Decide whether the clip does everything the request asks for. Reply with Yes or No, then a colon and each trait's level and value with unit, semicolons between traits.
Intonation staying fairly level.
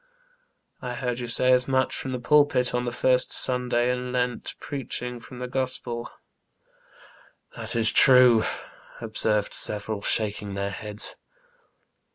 Yes: narrow, 2.1 semitones